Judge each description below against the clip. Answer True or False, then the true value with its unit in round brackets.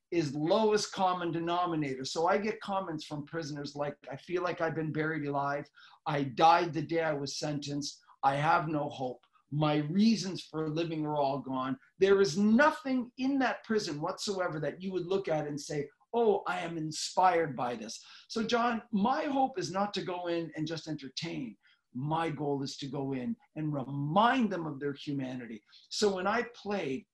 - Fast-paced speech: False (185 wpm)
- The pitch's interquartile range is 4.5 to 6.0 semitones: True (5.1 semitones)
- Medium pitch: True (165 Hz)